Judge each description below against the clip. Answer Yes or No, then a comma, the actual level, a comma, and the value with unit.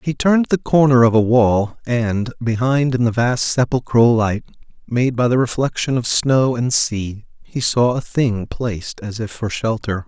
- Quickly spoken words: No, average, 185 wpm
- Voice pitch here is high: No, low, 120 Hz